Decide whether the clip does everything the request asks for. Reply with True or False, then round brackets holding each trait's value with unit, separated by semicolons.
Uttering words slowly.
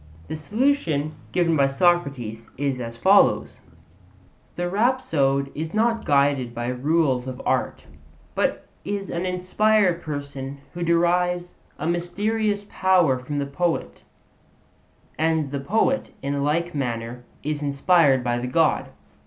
True (130 wpm)